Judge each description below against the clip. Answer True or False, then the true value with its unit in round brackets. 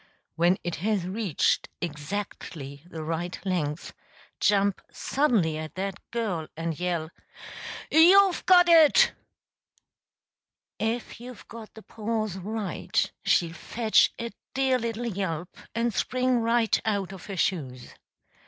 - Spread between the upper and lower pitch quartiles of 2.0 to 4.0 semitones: False (5.3 semitones)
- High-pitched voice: True (200 Hz)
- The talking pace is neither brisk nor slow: False (120 wpm)